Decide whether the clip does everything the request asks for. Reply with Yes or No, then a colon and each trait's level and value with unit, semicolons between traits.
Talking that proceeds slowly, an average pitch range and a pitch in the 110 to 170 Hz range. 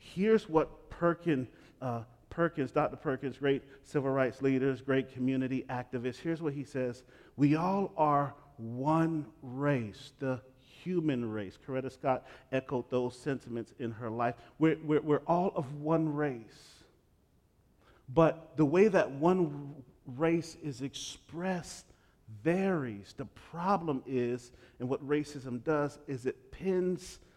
Yes: slow, 130 wpm; average, 3.8 semitones; medium, 140 Hz